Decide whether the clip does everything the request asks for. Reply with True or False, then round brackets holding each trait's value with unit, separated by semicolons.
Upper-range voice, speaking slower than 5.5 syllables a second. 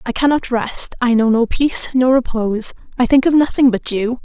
True (245 Hz; 5.3 syllables/s)